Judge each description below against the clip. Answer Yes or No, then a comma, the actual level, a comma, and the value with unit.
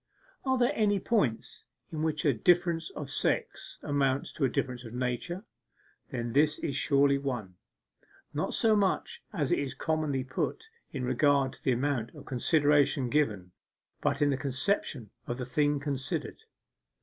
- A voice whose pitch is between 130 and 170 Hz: Yes, medium, 140 Hz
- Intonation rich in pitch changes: No, average, 3.5 semitones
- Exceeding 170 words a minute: No, average, 160 wpm